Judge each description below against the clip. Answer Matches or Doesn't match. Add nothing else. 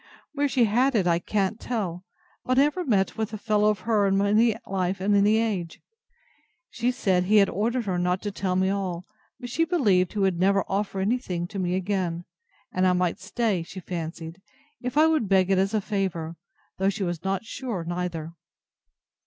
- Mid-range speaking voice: Doesn't match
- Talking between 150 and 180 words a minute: Doesn't match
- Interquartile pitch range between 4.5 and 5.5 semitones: Doesn't match